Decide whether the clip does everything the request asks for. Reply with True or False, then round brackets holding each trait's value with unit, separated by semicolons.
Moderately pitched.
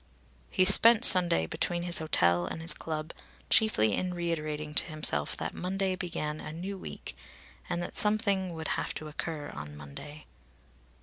True (165 Hz)